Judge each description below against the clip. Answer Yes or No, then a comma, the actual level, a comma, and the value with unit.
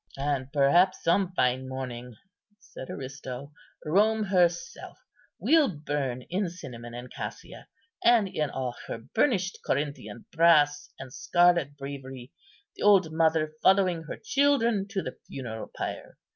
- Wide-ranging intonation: Yes, wide, 6.2 semitones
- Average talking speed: No, slow, 130 wpm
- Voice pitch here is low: No, medium, 150 Hz